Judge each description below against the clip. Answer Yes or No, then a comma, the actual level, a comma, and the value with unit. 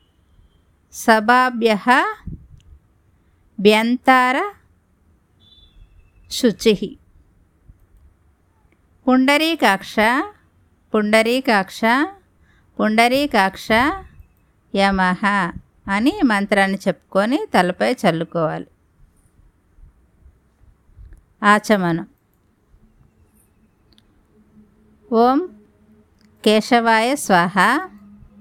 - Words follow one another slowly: Yes, slow, 30 wpm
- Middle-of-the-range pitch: Yes, medium, 180 Hz